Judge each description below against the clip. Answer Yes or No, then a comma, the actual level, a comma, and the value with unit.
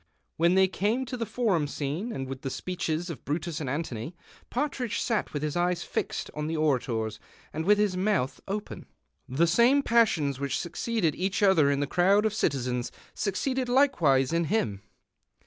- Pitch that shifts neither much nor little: No, wide, 6.9 semitones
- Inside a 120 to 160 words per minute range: No, average, 170 wpm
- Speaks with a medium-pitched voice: Yes, medium, 170 Hz